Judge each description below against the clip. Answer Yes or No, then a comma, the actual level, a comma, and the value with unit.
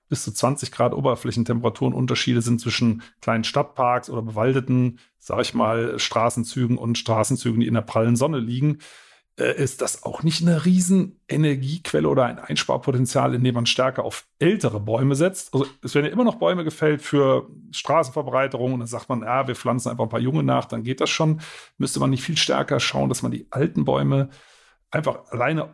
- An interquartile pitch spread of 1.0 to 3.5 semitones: No, average, 4.0 semitones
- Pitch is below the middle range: Yes, low, 125 Hz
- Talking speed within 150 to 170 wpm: No, average, 185 wpm